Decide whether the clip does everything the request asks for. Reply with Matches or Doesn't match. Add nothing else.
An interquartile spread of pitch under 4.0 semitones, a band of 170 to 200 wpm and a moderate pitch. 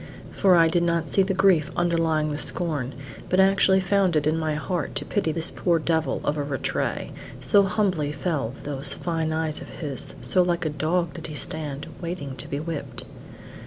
Matches